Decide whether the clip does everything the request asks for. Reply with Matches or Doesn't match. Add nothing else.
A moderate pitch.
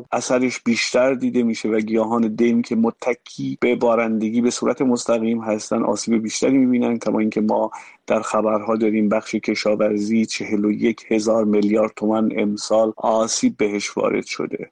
Doesn't match